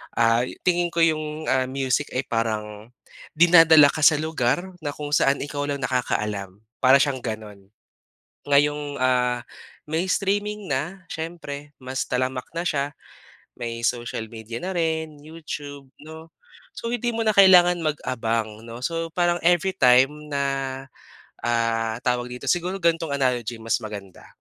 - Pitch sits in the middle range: Yes, medium, 145 Hz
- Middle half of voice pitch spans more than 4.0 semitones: Yes, average, 5.1 semitones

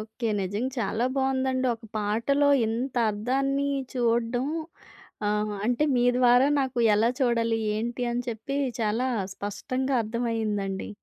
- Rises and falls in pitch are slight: No, average, 3.0 semitones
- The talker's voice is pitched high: Yes, high, 235 Hz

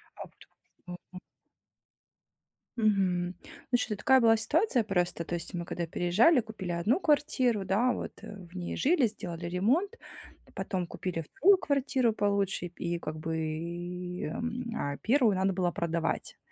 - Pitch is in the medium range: No, high, 195 Hz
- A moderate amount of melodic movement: No, wide, 5.8 semitones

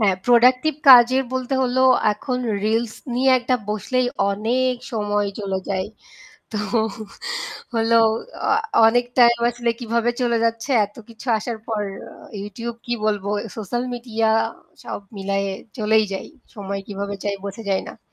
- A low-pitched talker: No, high, 225 Hz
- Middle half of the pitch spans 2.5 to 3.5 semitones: Yes, average, 2.8 semitones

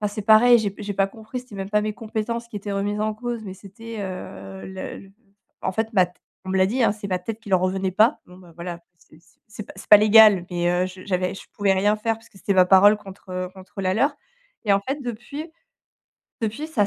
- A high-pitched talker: Yes, high, 205 Hz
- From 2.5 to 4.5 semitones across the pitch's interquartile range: Yes, average, 2.8 semitones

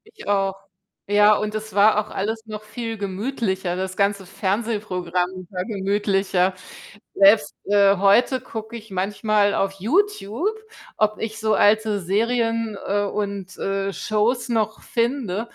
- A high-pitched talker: Yes, high, 205 Hz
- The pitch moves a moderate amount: No, narrow, 2.2 semitones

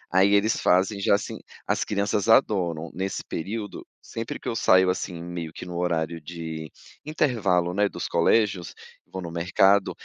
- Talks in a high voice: No, very low, 95 Hz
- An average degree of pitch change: Yes, average, 3.1 semitones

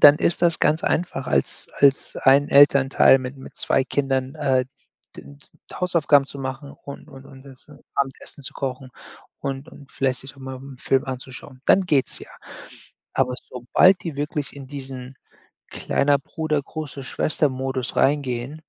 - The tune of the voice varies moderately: No, narrow, 1.6 semitones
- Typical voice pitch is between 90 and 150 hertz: Yes, low, 135 Hz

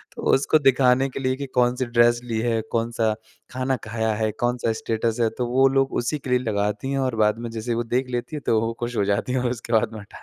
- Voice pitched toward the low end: Yes, low, 120 Hz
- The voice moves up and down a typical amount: No, narrow, 2.3 semitones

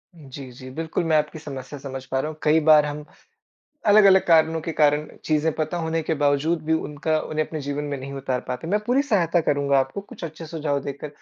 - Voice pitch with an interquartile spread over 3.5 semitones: No, narrow, 2.4 semitones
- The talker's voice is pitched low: No, medium, 155 Hz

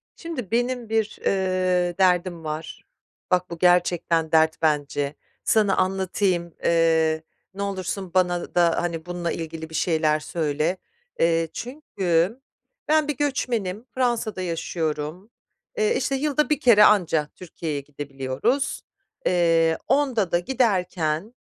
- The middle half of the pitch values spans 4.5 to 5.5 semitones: Yes, average, 4.8 semitones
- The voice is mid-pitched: Yes, medium, 180 Hz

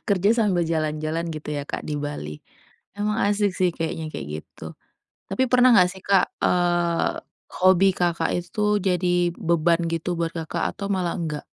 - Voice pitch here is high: No, medium, 175 Hz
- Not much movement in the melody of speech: No, average, 3.0 semitones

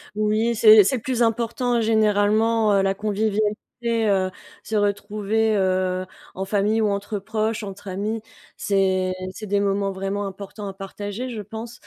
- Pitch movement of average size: No, narrow, 2.1 semitones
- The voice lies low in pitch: No, high, 210 Hz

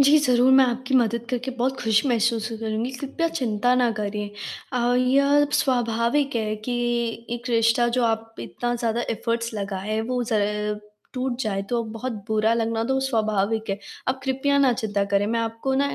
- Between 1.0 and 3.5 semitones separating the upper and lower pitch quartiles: Yes, average, 2.8 semitones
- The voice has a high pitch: Yes, high, 235 Hz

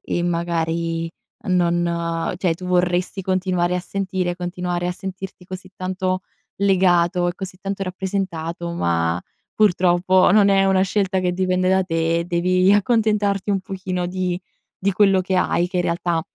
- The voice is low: No, medium, 180 Hz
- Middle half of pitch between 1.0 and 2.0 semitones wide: Yes, narrow, 1.5 semitones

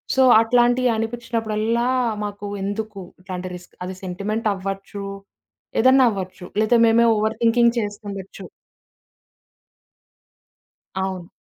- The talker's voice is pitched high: Yes, high, 215 Hz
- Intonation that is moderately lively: Yes, average, 3.0 semitones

